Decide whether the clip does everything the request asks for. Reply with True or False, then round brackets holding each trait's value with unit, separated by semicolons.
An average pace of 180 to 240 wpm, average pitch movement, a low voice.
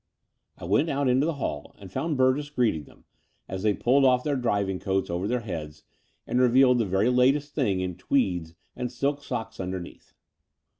False (185 wpm; 6.0 semitones; 120 Hz)